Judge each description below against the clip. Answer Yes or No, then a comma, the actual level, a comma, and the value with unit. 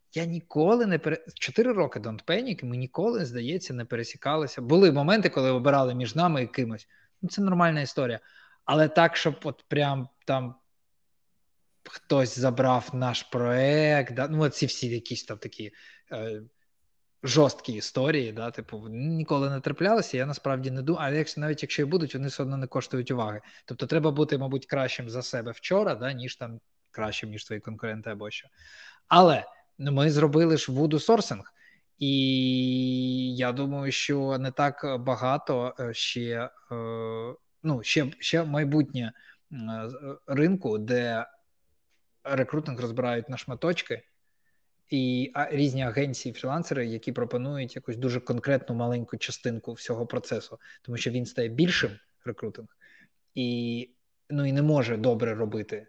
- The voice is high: No, low, 130 Hz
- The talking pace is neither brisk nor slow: Yes, average, 140 wpm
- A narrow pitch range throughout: No, average, 3.5 semitones